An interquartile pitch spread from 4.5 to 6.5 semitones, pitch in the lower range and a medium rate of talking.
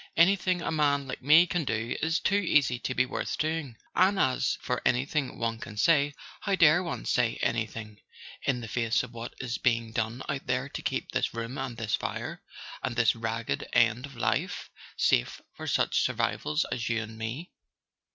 Yes: average, 4.8 semitones; low, 125 Hz; average, 190 wpm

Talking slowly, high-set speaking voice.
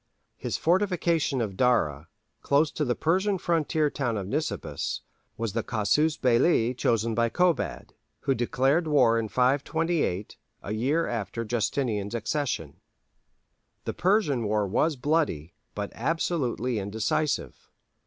No: slow, 125 wpm; low, 125 Hz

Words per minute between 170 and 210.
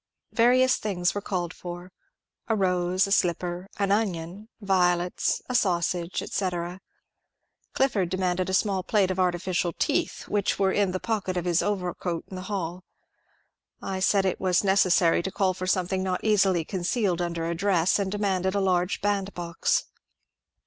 No: average, 160 wpm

